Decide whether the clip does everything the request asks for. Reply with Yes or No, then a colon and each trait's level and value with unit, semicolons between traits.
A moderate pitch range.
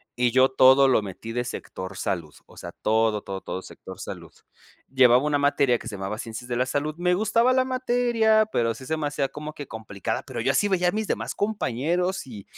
No: wide, 7.8 semitones